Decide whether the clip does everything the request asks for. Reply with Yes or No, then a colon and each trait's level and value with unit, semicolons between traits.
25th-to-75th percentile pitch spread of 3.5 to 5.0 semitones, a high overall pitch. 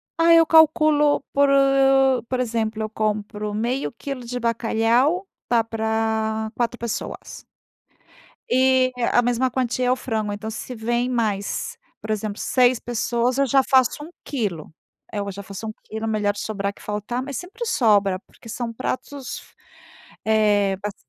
No: average, 3.0 semitones; high, 230 Hz